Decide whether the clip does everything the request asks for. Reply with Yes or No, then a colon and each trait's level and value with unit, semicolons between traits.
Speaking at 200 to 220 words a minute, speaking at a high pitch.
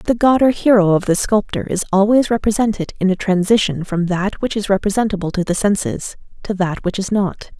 Yes: fast, 205 wpm; high, 200 Hz